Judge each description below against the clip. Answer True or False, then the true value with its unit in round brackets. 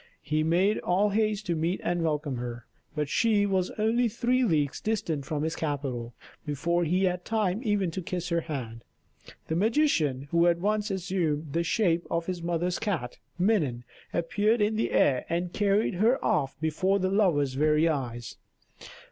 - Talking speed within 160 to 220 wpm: True (175 wpm)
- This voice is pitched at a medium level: True (175 Hz)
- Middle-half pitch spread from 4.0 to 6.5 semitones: True (5.1 semitones)